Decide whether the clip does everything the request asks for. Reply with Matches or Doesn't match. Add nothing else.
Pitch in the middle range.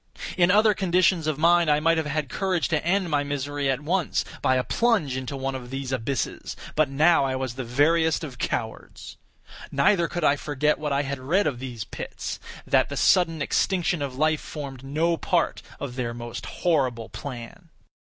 Matches